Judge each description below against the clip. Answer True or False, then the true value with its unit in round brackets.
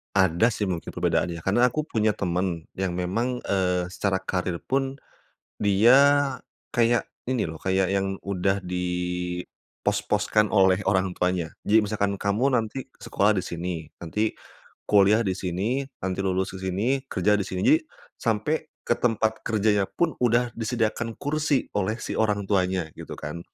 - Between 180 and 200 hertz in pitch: False (100 Hz)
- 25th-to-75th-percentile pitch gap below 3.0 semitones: False (3.7 semitones)